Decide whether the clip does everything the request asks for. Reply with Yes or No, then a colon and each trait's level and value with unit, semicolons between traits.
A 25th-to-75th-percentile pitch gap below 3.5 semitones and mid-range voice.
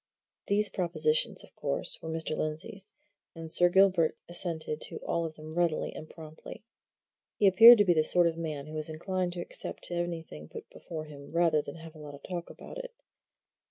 Yes: average, 2.9 semitones; medium, 165 Hz